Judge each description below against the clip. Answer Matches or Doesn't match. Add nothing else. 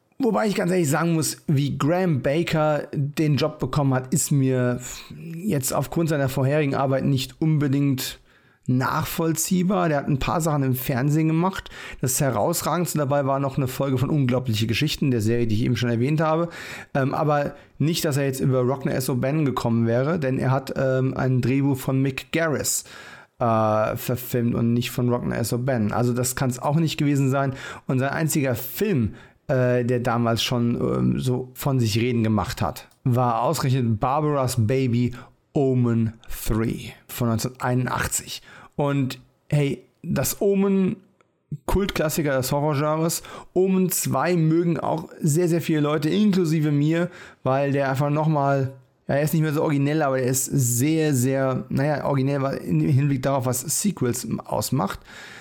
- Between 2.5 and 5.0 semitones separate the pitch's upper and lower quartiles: Matches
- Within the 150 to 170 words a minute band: Matches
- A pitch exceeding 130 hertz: Matches